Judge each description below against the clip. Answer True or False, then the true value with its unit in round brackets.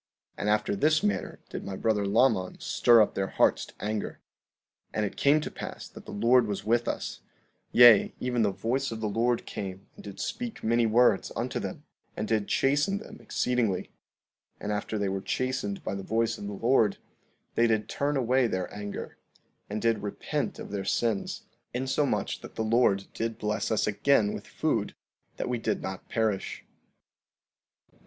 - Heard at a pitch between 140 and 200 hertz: False (110 Hz)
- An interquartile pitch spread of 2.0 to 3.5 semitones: True (3.2 semitones)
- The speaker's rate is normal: True (180 wpm)